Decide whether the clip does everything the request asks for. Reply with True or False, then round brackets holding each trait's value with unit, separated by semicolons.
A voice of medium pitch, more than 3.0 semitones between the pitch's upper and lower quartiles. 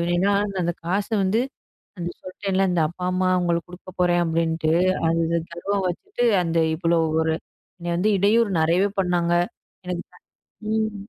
False (180 Hz; 2.6 semitones)